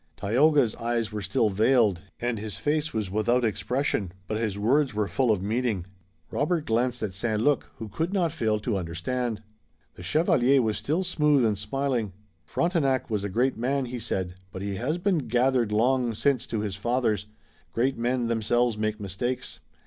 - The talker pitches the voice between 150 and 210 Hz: No, low, 115 Hz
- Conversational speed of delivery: Yes, average, 175 wpm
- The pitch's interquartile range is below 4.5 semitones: Yes, average, 4.0 semitones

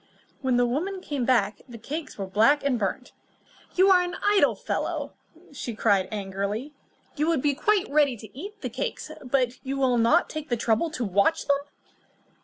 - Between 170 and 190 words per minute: Yes, average, 185 wpm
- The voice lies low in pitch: No, very high, 265 Hz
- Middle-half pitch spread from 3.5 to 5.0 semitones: No, wide, 5.5 semitones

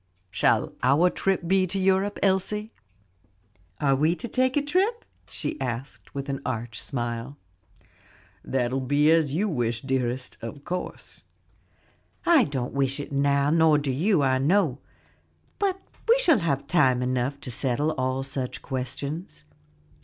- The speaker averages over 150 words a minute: No, average, 145 wpm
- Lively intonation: Yes, wide, 6.1 semitones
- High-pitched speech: No, medium, 140 Hz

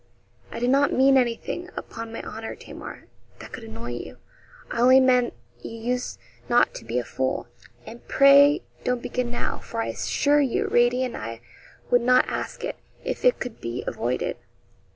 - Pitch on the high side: Yes, high, 240 Hz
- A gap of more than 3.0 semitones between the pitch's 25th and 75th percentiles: No, average, 2.7 semitones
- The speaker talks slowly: No, average, 175 wpm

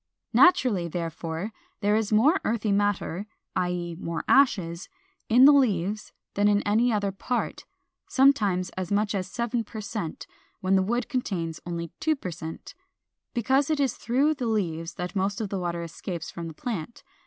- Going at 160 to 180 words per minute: Yes, average, 170 wpm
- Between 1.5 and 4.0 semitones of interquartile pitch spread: No, average, 5.2 semitones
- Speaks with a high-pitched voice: Yes, high, 205 Hz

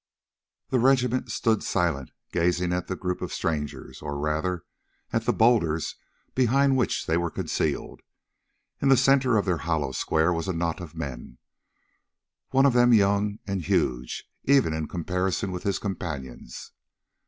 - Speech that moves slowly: No, average, 155 wpm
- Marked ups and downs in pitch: Yes, wide, 6.3 semitones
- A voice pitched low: Yes, very low, 90 Hz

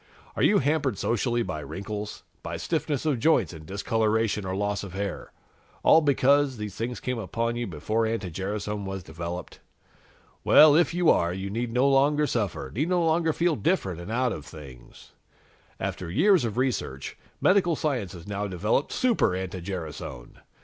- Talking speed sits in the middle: Yes, average, 170 wpm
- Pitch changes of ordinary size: No, wide, 7.0 semitones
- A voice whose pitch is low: Yes, low, 110 Hz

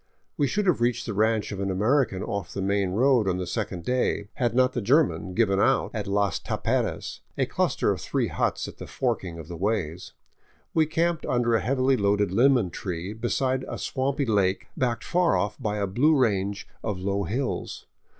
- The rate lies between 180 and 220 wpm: Yes, average, 200 wpm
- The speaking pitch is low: Yes, low, 110 Hz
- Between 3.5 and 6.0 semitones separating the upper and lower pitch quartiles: Yes, average, 4.8 semitones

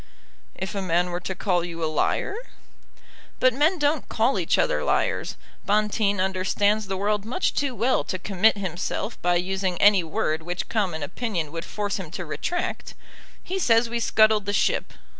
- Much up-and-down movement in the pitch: No, average, 4.0 semitones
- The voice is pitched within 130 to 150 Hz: No, high, 200 Hz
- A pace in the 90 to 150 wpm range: No, average, 175 wpm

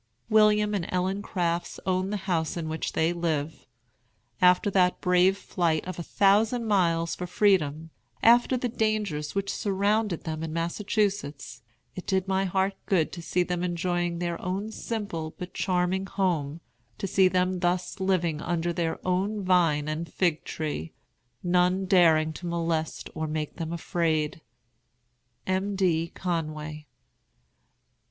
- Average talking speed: Yes, average, 145 wpm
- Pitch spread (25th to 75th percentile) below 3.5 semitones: Yes, average, 2.9 semitones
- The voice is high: No, medium, 180 Hz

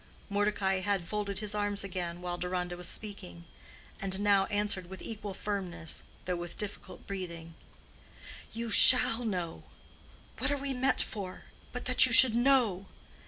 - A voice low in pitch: No, high, 200 Hz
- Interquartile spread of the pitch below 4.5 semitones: Yes, average, 3.0 semitones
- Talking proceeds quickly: No, average, 150 wpm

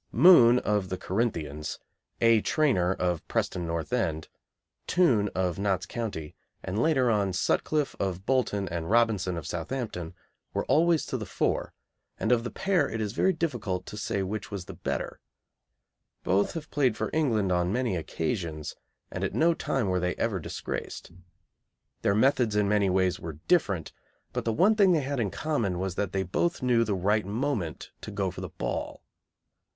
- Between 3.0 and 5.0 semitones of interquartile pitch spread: No, wide, 5.5 semitones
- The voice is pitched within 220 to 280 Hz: No, low, 105 Hz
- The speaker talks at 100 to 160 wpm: No, average, 175 wpm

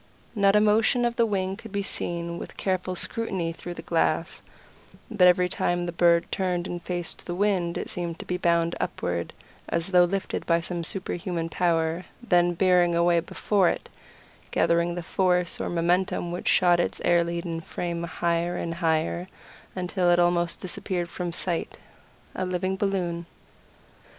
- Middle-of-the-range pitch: Yes, medium, 175 Hz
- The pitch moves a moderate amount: No, narrow, 1.6 semitones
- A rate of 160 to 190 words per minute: Yes, average, 165 wpm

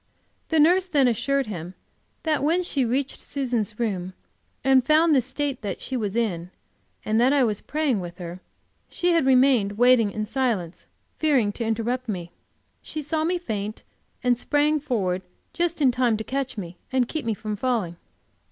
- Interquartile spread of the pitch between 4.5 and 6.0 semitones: Yes, average, 5.2 semitones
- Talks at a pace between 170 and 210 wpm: Yes, average, 175 wpm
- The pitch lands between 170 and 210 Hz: No, high, 245 Hz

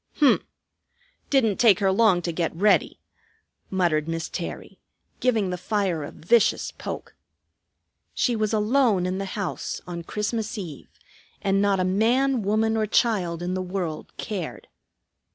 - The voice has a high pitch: Yes, high, 195 Hz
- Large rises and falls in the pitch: No, average, 3.7 semitones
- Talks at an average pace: Yes, average, 145 wpm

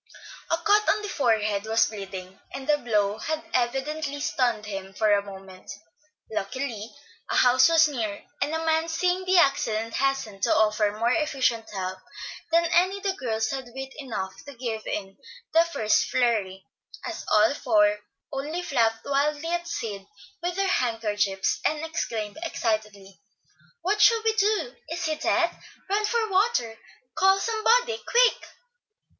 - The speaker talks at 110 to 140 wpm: No, average, 150 wpm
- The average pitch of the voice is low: No, very high, 265 Hz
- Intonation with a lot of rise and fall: Yes, wide, 7.9 semitones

